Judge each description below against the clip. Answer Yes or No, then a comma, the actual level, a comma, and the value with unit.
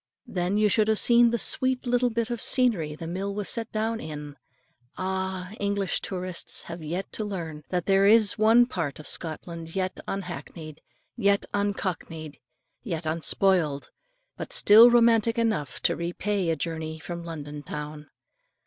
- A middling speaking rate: Yes, average, 155 wpm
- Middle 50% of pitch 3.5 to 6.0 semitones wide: Yes, average, 5.0 semitones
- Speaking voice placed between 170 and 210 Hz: Yes, high, 190 Hz